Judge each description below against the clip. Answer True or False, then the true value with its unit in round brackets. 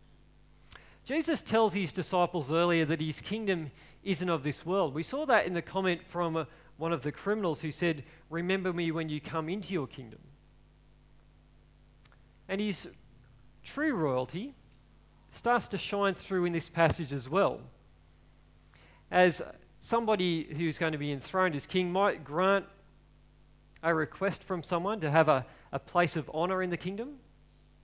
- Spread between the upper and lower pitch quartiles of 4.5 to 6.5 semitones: False (3.3 semitones)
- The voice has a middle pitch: True (175 Hz)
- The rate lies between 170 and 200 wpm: False (155 wpm)